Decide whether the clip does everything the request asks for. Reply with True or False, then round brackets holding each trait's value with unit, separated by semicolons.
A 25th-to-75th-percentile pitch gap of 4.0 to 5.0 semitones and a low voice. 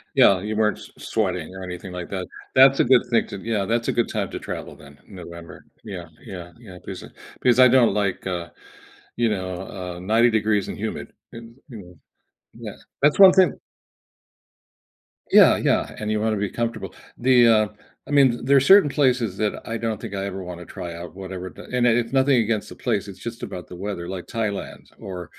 True (4.3 semitones; 105 Hz)